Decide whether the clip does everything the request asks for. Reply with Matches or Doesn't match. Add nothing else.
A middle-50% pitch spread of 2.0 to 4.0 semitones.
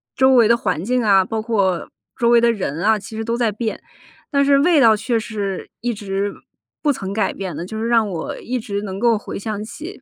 Matches